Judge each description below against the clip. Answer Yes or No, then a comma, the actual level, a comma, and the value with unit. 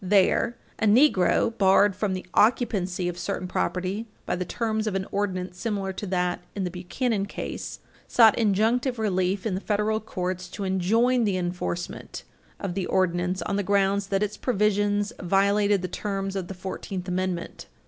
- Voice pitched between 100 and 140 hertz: No, high, 195 Hz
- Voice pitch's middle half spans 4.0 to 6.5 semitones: No, narrow, 2.5 semitones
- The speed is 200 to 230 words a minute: No, average, 170 wpm